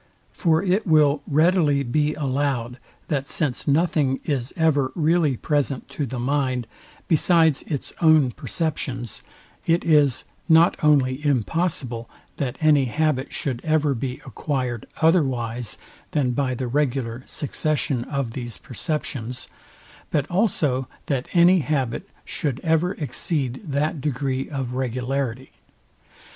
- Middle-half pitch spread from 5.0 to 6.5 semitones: No, average, 3.4 semitones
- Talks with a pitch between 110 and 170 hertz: Yes, medium, 140 Hz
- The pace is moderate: No, slow, 120 wpm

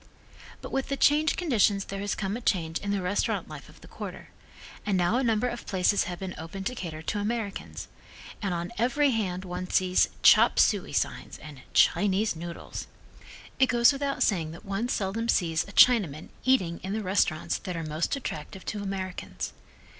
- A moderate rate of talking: Yes, average, 185 wpm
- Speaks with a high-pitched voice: Yes, high, 195 Hz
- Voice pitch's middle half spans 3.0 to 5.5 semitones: Yes, average, 4.5 semitones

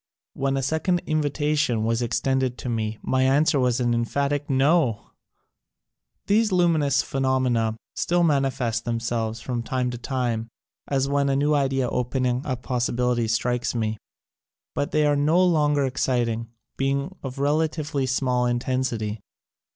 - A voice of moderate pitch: No, low, 130 Hz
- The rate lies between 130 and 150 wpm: Yes, average, 145 wpm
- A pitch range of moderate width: Yes, average, 3.2 semitones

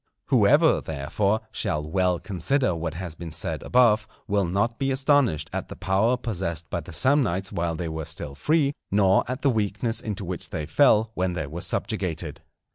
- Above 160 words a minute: Yes, average, 180 wpm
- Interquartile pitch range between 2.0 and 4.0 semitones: No, wide, 5.4 semitones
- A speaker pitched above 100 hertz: No, very low, 95 Hz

